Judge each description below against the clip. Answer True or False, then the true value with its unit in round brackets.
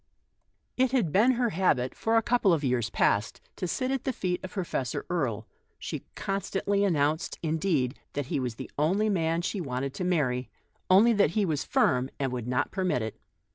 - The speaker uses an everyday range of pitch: False (7.3 semitones)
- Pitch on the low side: False (165 Hz)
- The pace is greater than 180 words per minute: True (195 wpm)